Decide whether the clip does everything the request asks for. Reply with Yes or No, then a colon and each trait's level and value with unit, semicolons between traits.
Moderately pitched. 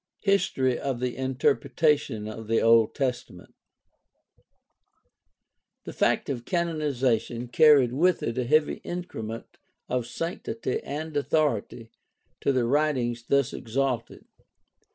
No: low, 130 Hz